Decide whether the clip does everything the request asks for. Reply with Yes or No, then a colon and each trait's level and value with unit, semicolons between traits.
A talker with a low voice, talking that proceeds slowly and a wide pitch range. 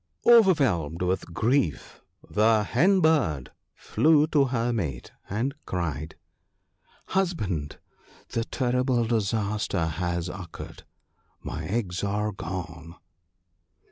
Yes: low, 105 Hz; slow, 105 wpm; wide, 6.9 semitones